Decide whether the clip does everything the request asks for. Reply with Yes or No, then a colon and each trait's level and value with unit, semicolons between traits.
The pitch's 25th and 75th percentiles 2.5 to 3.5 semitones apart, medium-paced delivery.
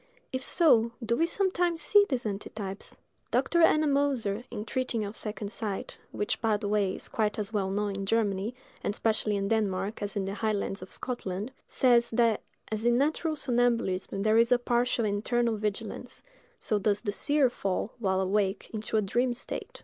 Yes: average, 3.2 semitones; average, 170 wpm